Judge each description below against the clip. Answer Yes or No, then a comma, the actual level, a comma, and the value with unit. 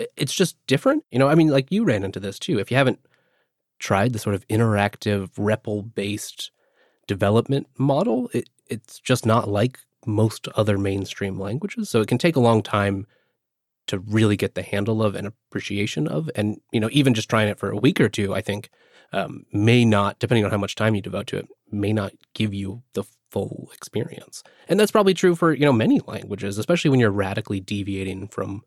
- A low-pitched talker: Yes, low, 110 Hz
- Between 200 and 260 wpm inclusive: Yes, fast, 205 wpm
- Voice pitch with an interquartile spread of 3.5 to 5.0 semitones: Yes, average, 4.0 semitones